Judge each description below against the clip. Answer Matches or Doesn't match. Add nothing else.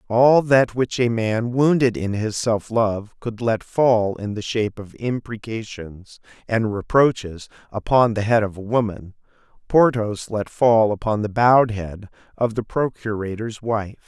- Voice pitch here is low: Matches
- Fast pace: Doesn't match